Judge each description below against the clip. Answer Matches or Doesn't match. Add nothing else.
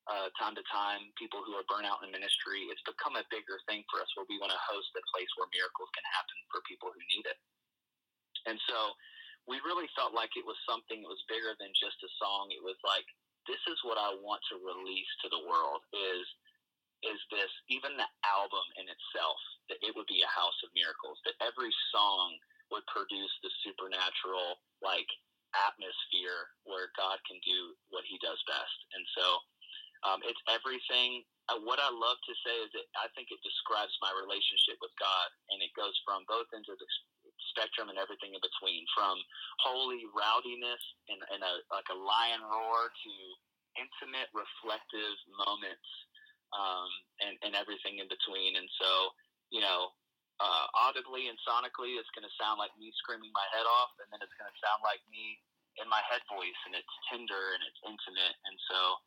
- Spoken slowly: Doesn't match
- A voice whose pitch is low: Doesn't match